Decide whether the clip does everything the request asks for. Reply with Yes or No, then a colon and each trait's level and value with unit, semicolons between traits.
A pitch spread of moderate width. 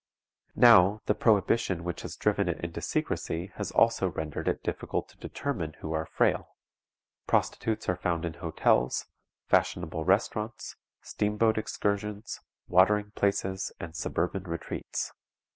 Yes: average, 3.8 semitones